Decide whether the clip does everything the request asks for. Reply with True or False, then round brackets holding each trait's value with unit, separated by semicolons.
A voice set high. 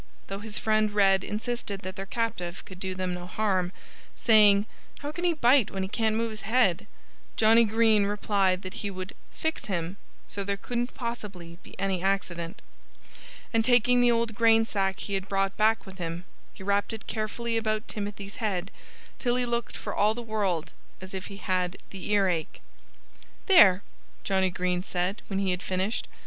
True (200 Hz)